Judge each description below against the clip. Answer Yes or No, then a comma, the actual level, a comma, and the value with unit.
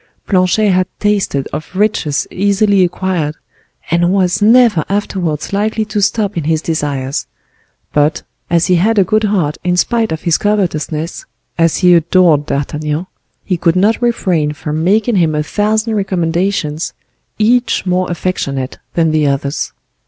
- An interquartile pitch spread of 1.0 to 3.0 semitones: No, average, 4.6 semitones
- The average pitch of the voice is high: No, medium, 180 Hz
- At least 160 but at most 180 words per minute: No, average, 145 wpm